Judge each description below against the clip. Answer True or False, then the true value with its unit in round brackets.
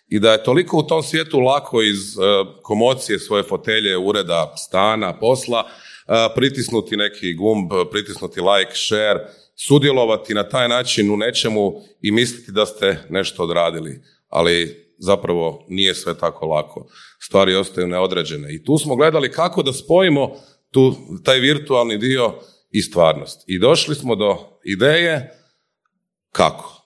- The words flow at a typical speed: True (135 wpm)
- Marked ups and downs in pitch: True (6.3 semitones)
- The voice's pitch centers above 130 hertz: False (120 Hz)